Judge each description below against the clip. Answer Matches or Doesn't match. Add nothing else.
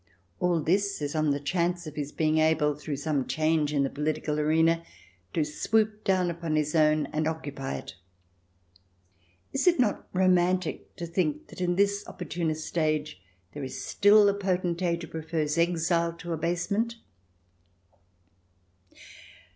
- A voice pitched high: Doesn't match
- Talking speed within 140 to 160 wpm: Matches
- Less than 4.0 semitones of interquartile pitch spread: Matches